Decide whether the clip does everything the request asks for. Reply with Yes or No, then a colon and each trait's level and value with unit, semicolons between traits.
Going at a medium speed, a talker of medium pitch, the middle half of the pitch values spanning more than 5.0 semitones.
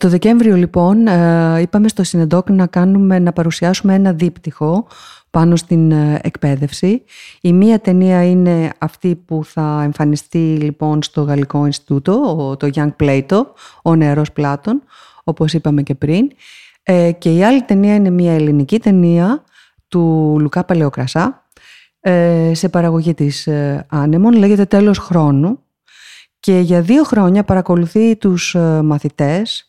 No: average, 125 wpm; medium, 170 Hz; average, 3.9 semitones